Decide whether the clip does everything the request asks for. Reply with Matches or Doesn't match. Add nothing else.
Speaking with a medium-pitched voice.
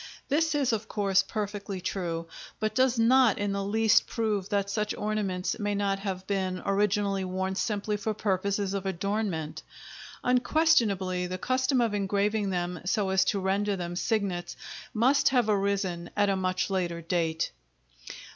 Doesn't match